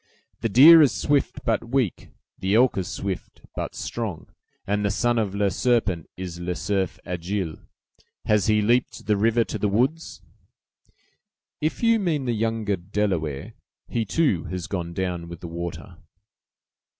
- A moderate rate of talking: Yes, average, 155 wpm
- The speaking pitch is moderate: No, low, 105 Hz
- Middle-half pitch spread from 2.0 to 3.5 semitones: No, average, 4.6 semitones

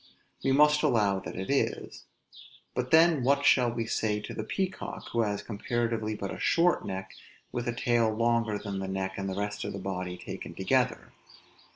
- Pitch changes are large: No, average, 4.2 semitones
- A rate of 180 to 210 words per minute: Yes, average, 190 wpm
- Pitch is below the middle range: Yes, low, 115 Hz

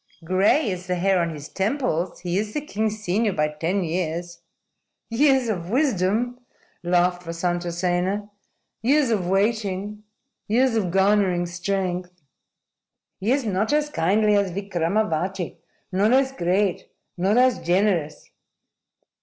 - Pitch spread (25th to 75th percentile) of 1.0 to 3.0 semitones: No, average, 3.7 semitones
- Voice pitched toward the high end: Yes, high, 195 Hz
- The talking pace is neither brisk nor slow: No, slow, 125 wpm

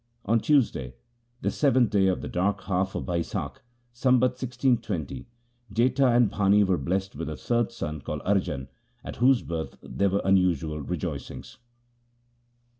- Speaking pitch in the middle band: No, low, 100 Hz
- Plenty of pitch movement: Yes, wide, 5.9 semitones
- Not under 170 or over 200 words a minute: No, average, 150 wpm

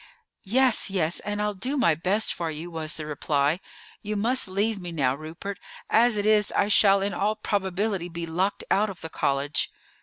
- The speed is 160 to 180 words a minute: No, average, 190 wpm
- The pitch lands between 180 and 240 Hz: Yes, high, 190 Hz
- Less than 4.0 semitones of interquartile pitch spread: No, average, 4.4 semitones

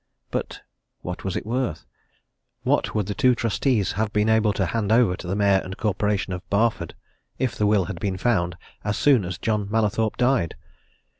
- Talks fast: No, average, 190 wpm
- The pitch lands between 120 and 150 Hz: No, low, 105 Hz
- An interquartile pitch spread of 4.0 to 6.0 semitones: No, average, 2.8 semitones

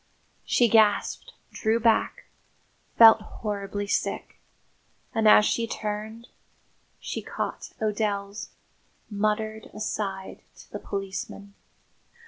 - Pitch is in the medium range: No, high, 210 Hz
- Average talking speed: No, slow, 95 wpm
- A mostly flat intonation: Yes, narrow, 1.5 semitones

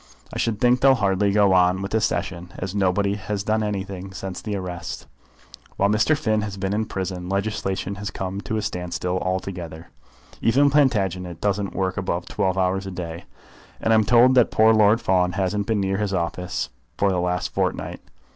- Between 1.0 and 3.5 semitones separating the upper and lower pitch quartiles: Yes, narrow, 2.5 semitones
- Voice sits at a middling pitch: No, very low, 95 Hz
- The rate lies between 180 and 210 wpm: Yes, average, 185 wpm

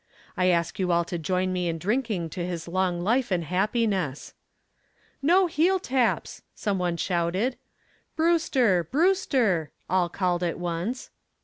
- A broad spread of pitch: Yes, wide, 6.1 semitones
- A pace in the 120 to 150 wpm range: Yes, average, 140 wpm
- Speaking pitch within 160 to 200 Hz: Yes, medium, 185 Hz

